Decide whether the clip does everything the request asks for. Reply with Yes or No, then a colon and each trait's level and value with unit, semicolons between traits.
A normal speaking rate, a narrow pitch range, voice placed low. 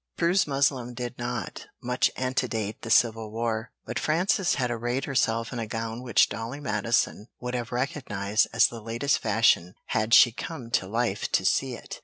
Yes: average, 175 wpm; narrow, 2.3 semitones; low, 120 Hz